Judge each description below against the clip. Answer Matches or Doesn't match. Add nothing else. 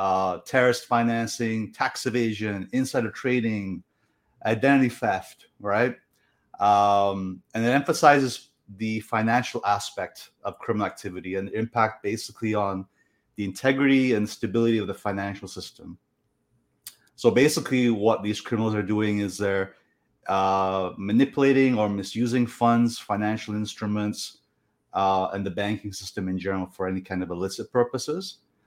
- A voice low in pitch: Matches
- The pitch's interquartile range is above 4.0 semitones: Doesn't match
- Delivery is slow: Matches